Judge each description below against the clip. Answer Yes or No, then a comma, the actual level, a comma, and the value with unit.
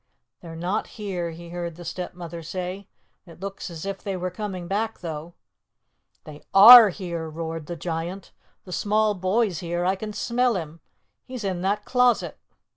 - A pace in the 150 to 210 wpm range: Yes, average, 165 wpm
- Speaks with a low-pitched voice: No, medium, 180 Hz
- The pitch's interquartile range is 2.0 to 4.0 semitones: Yes, average, 3.2 semitones